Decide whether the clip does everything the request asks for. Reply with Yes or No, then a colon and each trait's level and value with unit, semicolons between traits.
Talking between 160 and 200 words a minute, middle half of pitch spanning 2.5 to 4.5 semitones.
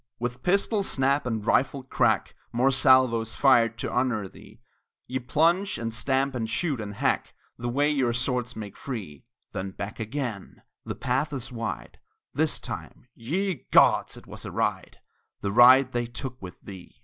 Yes: average, 165 wpm; average, 3.1 semitones